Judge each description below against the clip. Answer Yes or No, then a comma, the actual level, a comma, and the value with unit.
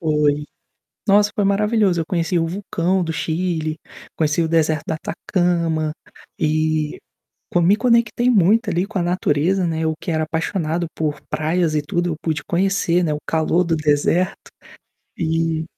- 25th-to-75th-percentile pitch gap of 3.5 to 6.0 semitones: No, average, 2.8 semitones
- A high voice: No, medium, 165 Hz